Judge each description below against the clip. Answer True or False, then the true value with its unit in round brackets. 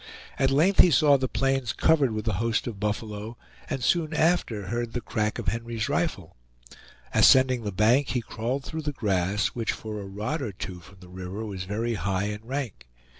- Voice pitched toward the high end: False (115 Hz)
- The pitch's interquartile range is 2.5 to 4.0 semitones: False (4.6 semitones)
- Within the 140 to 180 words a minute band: False (195 wpm)